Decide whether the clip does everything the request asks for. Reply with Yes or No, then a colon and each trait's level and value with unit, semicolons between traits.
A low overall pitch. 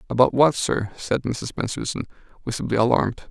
Yes: low, 120 Hz